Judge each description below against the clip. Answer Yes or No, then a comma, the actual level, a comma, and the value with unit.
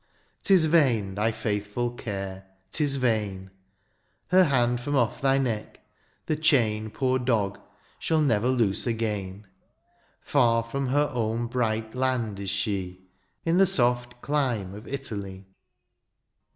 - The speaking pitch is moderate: No, low, 120 Hz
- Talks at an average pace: No, slow, 125 wpm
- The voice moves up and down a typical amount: Yes, average, 4.4 semitones